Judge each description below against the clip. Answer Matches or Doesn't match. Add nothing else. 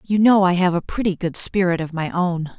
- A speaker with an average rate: Doesn't match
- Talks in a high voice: Doesn't match